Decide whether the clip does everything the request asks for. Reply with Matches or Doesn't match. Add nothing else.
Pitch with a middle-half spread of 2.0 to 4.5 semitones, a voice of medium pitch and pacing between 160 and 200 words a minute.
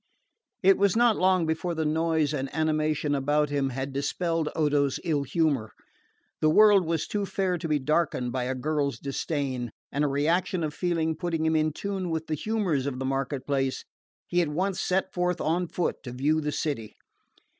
Matches